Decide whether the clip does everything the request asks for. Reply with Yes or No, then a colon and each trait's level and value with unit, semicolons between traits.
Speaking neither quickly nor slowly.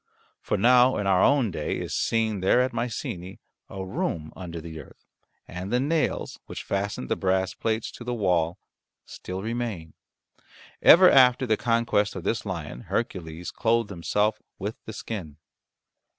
Yes: average, 155 wpm